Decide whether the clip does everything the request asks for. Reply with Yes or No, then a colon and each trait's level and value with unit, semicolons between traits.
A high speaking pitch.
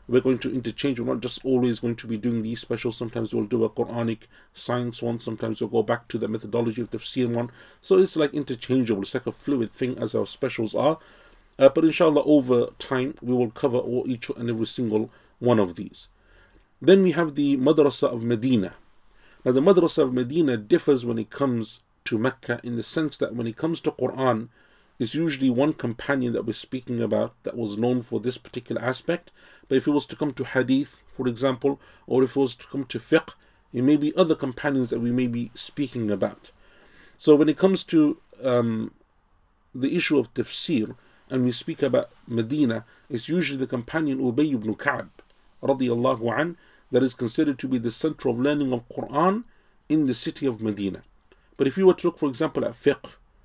No: low, 125 Hz